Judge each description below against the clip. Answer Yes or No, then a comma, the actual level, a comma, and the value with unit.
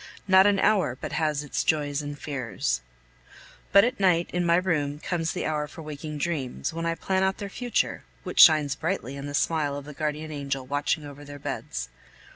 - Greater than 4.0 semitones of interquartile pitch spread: No, average, 3.2 semitones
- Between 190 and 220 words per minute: Yes, average, 200 wpm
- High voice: No, medium, 150 Hz